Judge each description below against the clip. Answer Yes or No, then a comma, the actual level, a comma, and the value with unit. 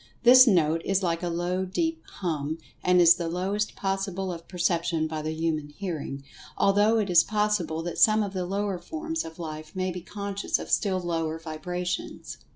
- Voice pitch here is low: No, medium, 180 Hz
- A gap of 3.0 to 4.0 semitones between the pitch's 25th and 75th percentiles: Yes, average, 3.3 semitones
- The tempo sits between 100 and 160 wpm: No, average, 185 wpm